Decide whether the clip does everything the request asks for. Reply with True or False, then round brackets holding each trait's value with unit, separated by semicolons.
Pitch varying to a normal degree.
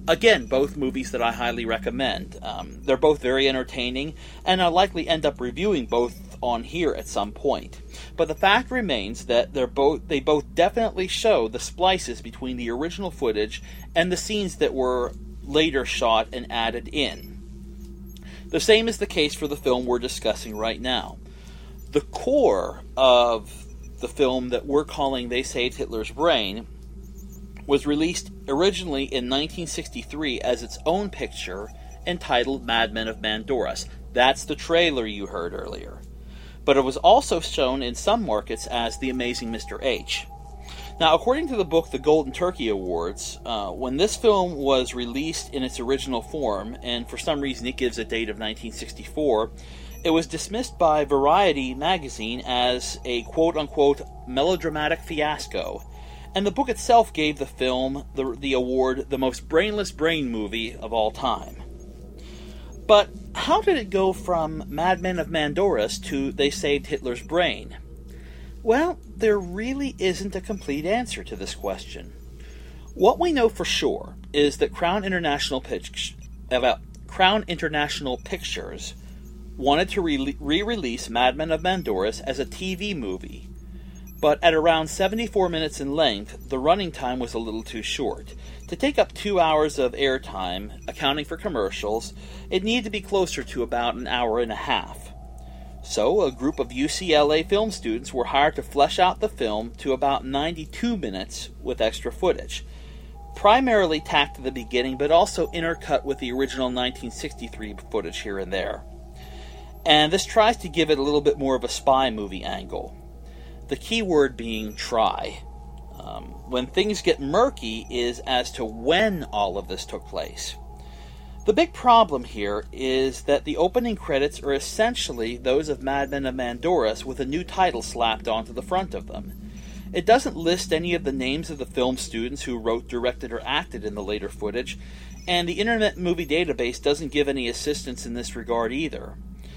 False (7.6 semitones)